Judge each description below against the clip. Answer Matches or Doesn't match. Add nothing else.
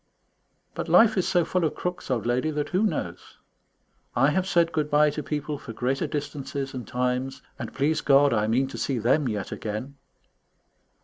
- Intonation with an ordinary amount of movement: Matches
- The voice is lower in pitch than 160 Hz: Matches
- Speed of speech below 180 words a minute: Doesn't match